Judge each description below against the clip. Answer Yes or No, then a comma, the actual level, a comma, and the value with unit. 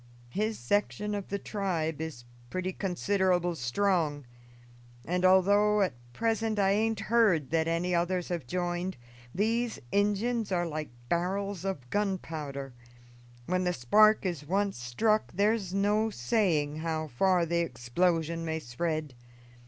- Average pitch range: Yes, average, 4.2 semitones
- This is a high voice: No, medium, 180 Hz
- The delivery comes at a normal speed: No, slow, 130 wpm